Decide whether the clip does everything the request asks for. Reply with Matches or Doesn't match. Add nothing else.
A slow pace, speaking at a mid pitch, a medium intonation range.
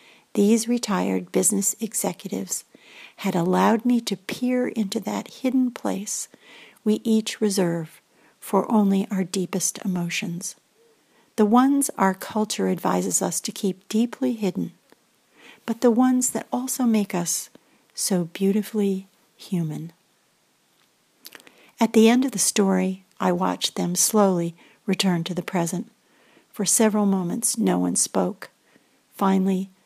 Doesn't match